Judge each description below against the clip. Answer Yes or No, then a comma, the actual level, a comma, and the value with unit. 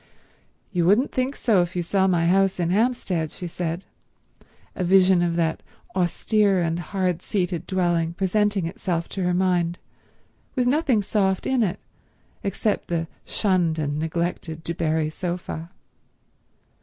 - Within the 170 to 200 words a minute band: No, average, 145 wpm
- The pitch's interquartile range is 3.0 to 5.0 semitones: No, narrow, 2.5 semitones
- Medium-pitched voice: Yes, medium, 180 Hz